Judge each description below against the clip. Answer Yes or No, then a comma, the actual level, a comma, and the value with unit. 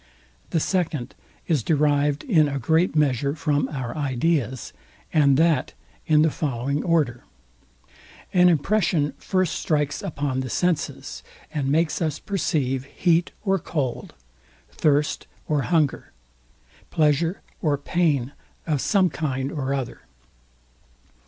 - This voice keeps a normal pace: No, slow, 120 wpm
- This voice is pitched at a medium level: Yes, medium, 150 Hz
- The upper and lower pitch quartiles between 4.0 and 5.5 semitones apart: No, average, 3.2 semitones